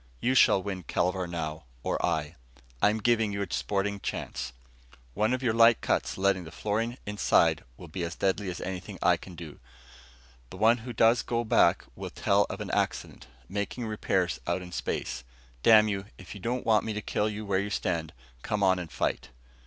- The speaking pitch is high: No, low, 100 Hz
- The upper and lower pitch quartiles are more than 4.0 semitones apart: No, average, 3.3 semitones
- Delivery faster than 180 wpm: Yes, average, 190 wpm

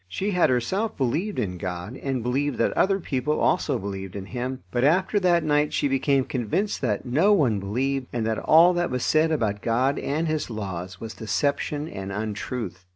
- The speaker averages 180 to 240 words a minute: Yes, average, 190 wpm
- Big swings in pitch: Yes, wide, 6.1 semitones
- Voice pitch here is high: No, low, 130 Hz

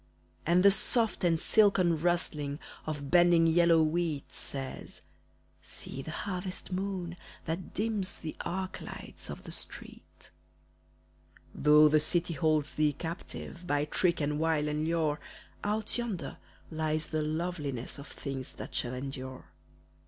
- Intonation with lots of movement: No, average, 3.0 semitones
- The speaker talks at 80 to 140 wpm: Yes, slow, 135 wpm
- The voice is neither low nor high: Yes, medium, 160 Hz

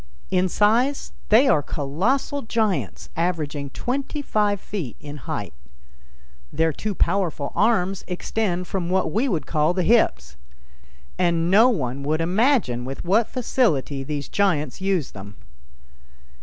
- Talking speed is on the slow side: Yes, slow, 130 wpm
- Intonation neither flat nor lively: No, wide, 6.4 semitones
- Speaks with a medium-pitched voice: Yes, medium, 180 Hz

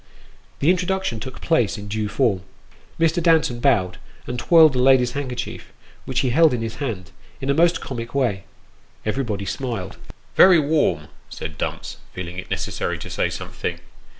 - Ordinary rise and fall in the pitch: No, wide, 6.3 semitones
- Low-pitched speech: Yes, low, 125 Hz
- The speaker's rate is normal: Yes, average, 165 wpm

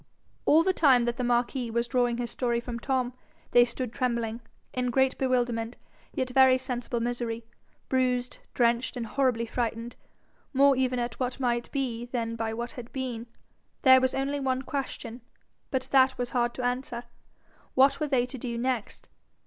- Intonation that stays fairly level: Yes, narrow, 1.6 semitones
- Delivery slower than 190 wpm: Yes, average, 170 wpm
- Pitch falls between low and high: No, high, 245 Hz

